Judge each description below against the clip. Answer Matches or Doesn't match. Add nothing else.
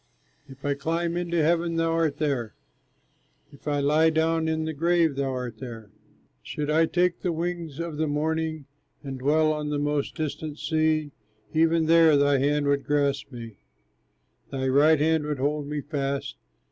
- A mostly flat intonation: Matches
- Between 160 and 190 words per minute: Matches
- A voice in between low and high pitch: Matches